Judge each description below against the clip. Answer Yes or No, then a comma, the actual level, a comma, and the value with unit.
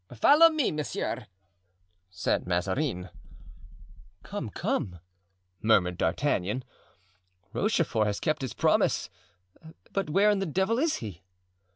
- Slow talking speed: Yes, slow, 105 wpm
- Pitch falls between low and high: Yes, medium, 145 Hz